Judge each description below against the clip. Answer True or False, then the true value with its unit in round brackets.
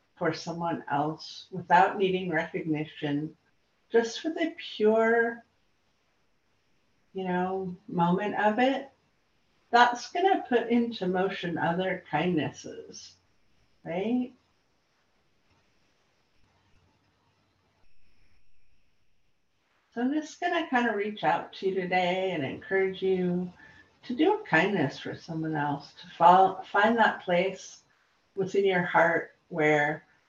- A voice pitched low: False (180 Hz)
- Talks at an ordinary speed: False (105 wpm)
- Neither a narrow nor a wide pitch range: False (6.1 semitones)